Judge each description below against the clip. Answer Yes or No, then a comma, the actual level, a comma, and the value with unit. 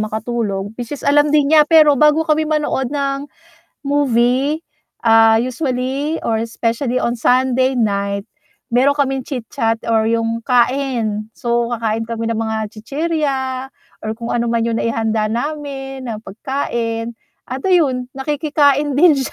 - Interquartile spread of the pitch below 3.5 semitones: No, average, 3.8 semitones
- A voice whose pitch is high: Yes, very high, 255 Hz